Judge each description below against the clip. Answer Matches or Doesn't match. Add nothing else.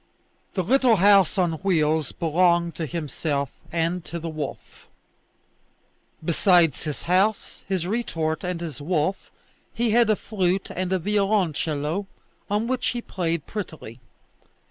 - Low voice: Doesn't match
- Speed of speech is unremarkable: Doesn't match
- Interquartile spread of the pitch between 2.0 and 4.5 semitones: Matches